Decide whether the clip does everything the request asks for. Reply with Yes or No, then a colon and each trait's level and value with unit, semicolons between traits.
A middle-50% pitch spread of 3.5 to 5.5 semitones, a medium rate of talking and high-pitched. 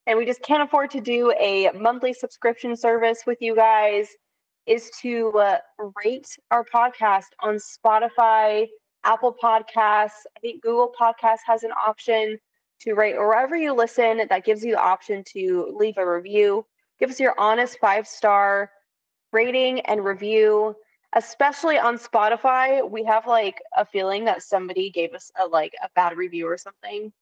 No: narrow, 2.6 semitones; average, 160 wpm; high, 225 Hz